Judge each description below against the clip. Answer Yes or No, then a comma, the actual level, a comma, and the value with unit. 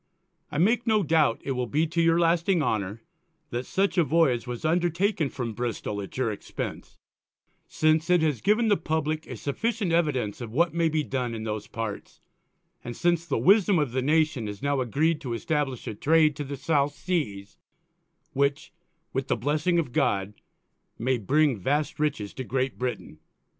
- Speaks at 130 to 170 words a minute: No, average, 180 wpm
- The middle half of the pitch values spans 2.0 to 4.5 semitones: No, average, 5.3 semitones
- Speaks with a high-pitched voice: No, medium, 145 Hz